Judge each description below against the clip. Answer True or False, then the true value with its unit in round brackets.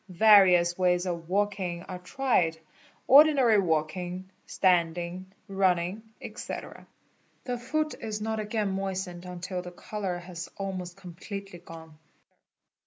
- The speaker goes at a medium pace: False (115 wpm)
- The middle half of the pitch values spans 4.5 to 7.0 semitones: False (2.7 semitones)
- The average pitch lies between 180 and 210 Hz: True (185 Hz)